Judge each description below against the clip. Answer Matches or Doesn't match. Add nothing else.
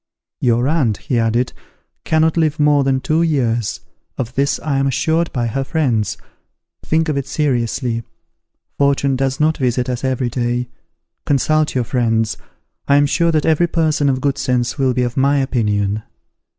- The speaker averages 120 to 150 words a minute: Doesn't match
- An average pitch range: Matches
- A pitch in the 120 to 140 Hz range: Matches